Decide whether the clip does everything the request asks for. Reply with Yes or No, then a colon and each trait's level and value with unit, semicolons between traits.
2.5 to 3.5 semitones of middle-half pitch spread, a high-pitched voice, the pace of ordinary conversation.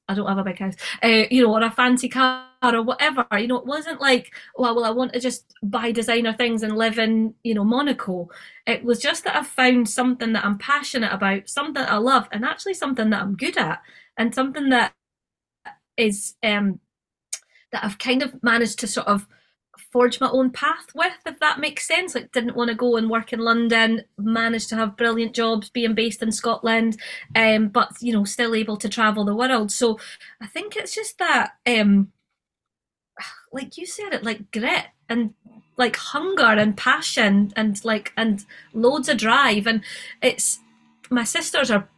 Yes: average, 2.8 semitones; high, 230 Hz; average, 195 wpm